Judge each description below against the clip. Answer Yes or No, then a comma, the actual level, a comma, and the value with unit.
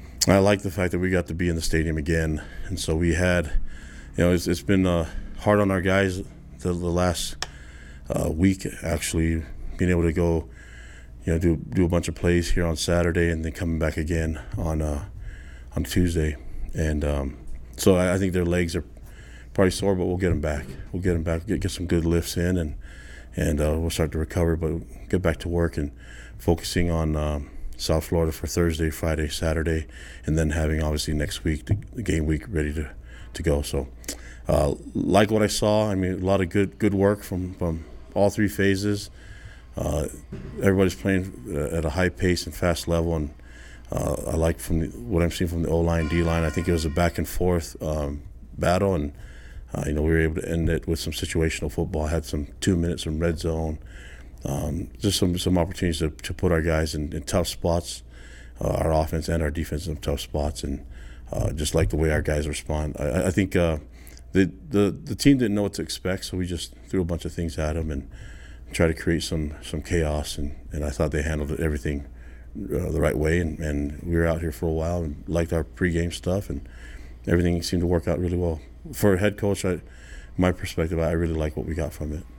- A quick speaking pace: Yes, fast, 220 wpm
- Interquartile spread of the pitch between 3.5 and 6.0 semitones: No, average, 2.9 semitones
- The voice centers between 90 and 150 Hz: No, very low, 80 Hz